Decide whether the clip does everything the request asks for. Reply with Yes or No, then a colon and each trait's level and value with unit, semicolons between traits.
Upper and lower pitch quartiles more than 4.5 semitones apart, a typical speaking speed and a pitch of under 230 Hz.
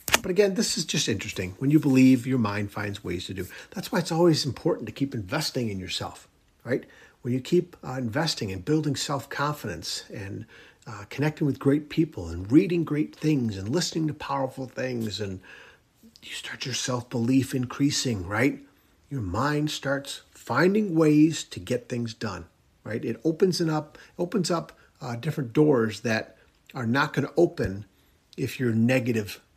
Yes: wide, 5.4 semitones; average, 170 wpm; low, 135 Hz